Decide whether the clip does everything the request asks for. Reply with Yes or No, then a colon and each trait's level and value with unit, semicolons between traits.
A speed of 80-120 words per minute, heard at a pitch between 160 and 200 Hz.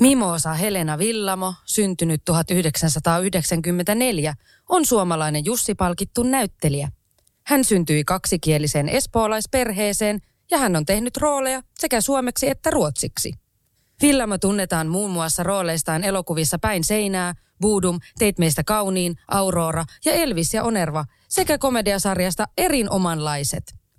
Yes: average, 105 wpm; high, 190 Hz